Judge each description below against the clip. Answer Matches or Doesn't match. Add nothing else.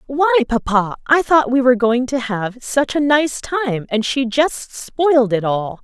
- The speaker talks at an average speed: Matches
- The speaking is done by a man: Doesn't match